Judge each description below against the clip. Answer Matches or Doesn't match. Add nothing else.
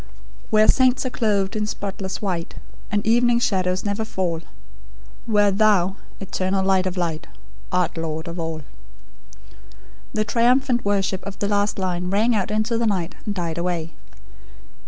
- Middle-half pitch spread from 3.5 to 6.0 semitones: Doesn't match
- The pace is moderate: Matches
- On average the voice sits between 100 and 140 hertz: Doesn't match